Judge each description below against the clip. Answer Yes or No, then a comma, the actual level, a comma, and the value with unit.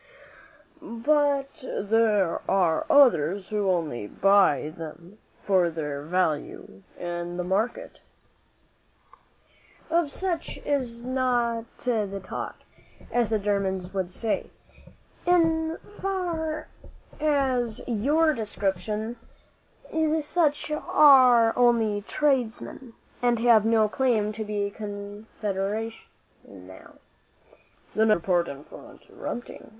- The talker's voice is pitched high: Yes, high, 220 Hz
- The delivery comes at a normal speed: No, slow, 105 wpm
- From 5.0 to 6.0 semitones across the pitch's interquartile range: Yes, wide, 5.5 semitones